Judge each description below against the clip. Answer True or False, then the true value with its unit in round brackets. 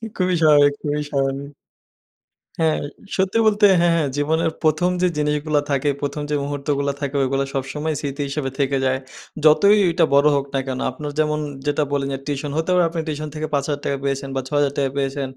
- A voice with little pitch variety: True (2.0 semitones)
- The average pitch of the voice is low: False (145 Hz)